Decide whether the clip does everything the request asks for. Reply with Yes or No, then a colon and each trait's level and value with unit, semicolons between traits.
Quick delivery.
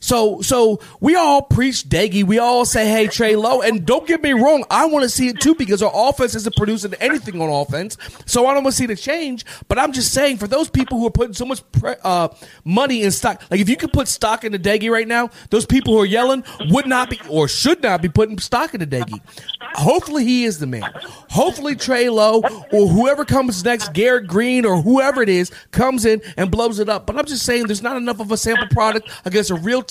Yes: fast, 245 wpm